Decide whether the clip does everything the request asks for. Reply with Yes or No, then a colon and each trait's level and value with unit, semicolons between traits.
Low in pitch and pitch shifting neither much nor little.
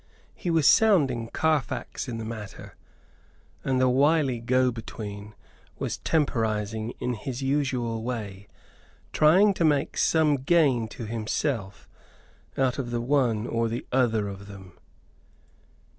Yes: low, 120 Hz; average, 4.1 semitones